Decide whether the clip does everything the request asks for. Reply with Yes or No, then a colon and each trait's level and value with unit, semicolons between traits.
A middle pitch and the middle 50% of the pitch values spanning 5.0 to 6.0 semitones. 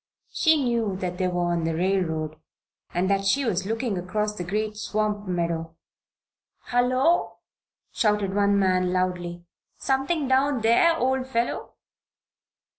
No: high, 205 Hz; average, 5.3 semitones